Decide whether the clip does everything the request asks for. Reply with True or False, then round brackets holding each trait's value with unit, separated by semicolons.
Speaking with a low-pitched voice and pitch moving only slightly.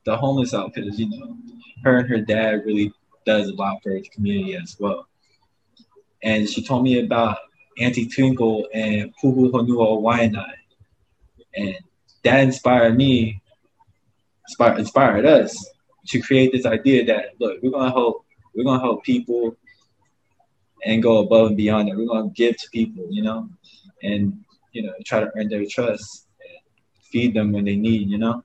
False (115 Hz; 3.5 semitones)